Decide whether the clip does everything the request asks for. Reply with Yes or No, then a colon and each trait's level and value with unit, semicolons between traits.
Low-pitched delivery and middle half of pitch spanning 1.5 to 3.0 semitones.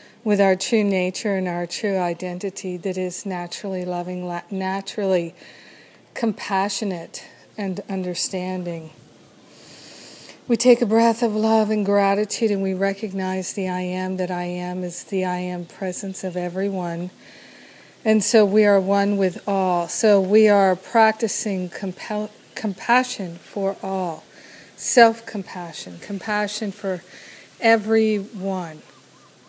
No: high, 195 Hz; narrow, 2.5 semitones